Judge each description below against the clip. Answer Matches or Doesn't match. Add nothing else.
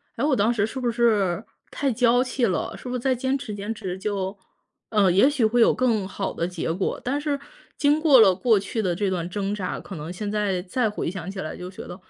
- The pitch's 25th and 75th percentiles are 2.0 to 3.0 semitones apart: Doesn't match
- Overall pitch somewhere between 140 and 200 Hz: Doesn't match